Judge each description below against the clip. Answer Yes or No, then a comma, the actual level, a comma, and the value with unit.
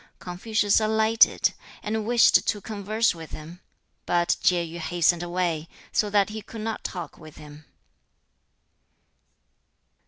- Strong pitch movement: No, average, 4.2 semitones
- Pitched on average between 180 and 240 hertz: Yes, medium, 185 Hz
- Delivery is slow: Yes, slow, 130 wpm